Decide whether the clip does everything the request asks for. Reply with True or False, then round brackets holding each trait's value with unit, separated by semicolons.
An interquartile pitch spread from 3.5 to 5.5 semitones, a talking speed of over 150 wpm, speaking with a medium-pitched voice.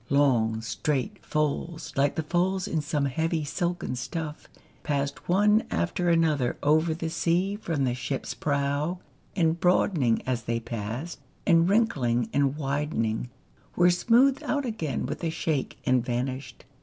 False (4.8 semitones; 145 wpm; 150 Hz)